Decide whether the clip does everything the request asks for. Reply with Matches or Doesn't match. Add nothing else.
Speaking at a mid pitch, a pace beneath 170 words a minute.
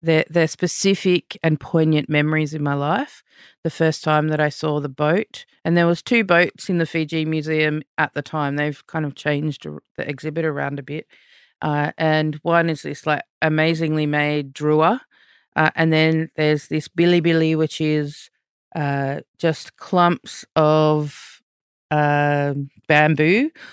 Matches